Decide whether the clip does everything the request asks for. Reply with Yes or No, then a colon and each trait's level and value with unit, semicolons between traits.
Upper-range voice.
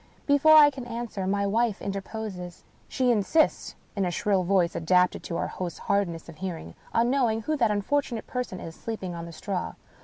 Yes: high, 200 Hz